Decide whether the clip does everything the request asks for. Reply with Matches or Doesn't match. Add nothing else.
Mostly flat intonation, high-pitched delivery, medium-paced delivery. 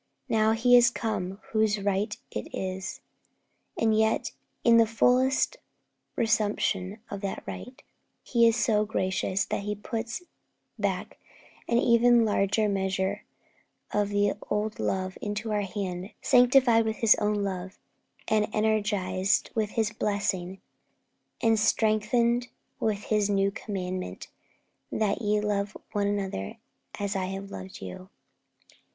Doesn't match